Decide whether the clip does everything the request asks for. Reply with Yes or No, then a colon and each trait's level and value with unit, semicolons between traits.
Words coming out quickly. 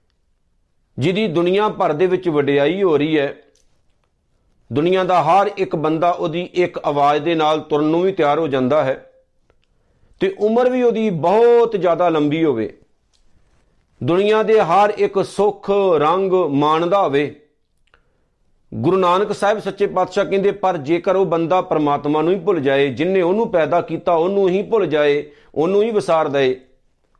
No: average, 150 wpm